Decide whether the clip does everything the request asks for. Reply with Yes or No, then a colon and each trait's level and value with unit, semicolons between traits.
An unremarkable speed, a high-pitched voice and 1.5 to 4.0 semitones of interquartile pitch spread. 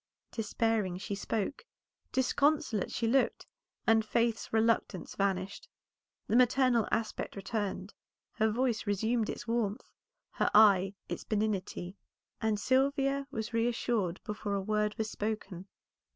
No: slow, 120 wpm; high, 220 Hz; average, 2.7 semitones